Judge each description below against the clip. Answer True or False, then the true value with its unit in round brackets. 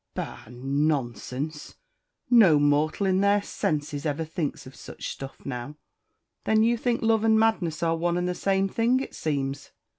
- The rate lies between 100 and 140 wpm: False (160 wpm)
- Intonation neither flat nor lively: False (5.9 semitones)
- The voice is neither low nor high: True (160 Hz)